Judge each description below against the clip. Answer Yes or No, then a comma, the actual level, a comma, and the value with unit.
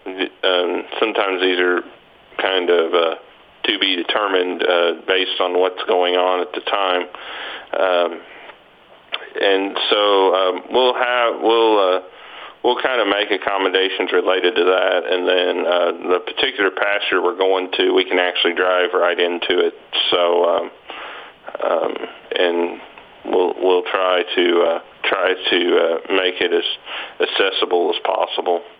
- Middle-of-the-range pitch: No, very low, 95 Hz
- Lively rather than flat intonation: Yes, wide, 5.8 semitones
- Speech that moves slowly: No, average, 145 wpm